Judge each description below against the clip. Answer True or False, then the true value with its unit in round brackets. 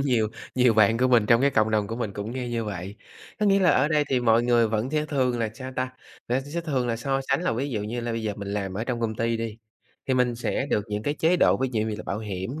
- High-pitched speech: False (120 Hz)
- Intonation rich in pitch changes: False (3.2 semitones)